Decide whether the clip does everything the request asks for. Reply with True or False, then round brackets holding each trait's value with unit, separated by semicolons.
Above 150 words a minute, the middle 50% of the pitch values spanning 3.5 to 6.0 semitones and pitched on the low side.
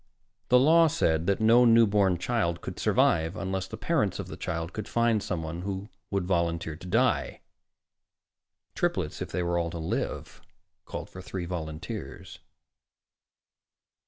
False (145 wpm; 4.7 semitones; 95 Hz)